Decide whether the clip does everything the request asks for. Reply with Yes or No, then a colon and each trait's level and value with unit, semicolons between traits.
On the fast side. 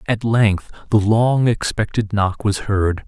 No: average, 155 wpm